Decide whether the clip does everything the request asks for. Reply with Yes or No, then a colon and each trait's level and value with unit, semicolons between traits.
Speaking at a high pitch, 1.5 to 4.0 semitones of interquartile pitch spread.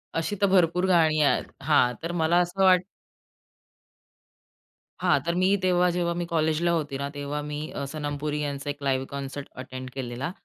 No: medium, 155 Hz; average, 3.5 semitones